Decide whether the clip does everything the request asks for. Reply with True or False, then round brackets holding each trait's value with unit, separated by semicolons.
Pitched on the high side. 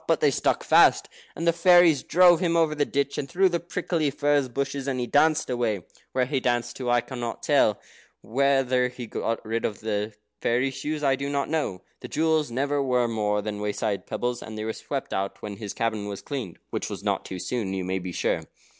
False (125 Hz)